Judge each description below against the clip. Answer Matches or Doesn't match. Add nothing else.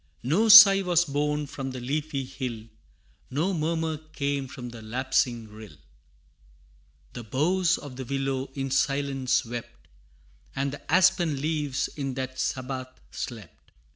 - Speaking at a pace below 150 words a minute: Matches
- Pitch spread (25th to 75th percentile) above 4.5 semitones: Doesn't match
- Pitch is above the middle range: Doesn't match